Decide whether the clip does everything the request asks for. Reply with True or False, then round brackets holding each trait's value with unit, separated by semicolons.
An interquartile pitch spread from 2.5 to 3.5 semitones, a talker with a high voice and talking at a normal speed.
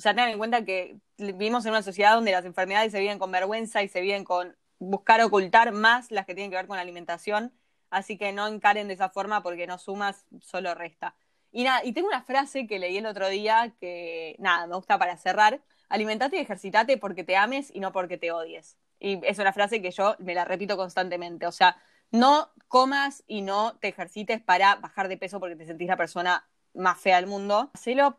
False (3.2 semitones; 200 Hz; 220 wpm)